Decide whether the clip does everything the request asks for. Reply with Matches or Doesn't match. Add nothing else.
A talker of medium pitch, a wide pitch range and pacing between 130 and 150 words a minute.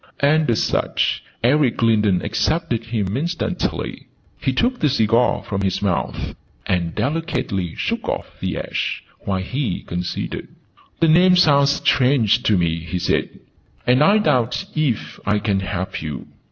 Doesn't match